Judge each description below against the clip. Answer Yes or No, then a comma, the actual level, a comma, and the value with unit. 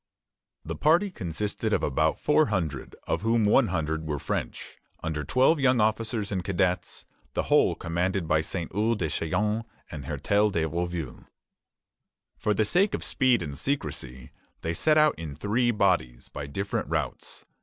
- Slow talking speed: No, average, 160 wpm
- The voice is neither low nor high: No, very low, 95 Hz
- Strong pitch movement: Yes, wide, 6.2 semitones